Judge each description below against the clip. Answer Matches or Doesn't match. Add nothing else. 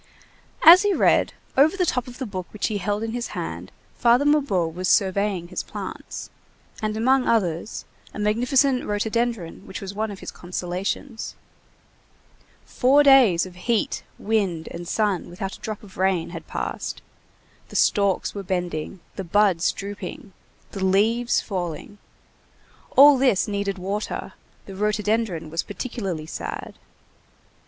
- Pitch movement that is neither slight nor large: Matches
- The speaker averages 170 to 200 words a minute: Doesn't match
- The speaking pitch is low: Doesn't match